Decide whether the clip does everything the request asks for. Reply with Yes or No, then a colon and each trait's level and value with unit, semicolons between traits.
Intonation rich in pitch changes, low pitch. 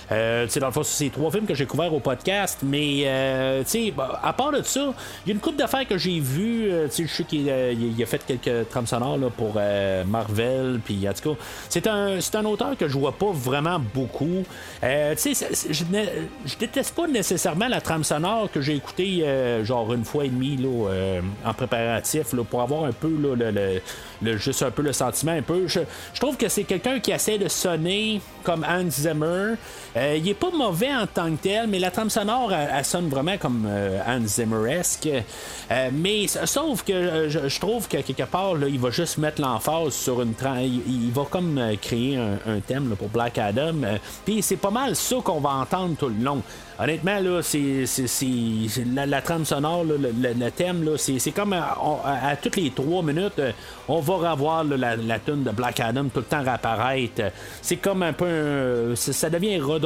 No: wide, 6.6 semitones; medium, 145 Hz